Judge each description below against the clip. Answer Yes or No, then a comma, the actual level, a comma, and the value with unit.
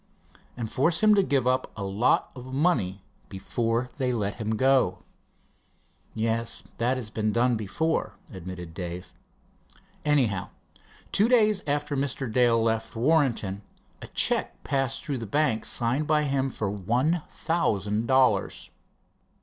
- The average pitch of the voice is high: No, low, 125 Hz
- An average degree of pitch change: Yes, average, 4.7 semitones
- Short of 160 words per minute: Yes, slow, 135 wpm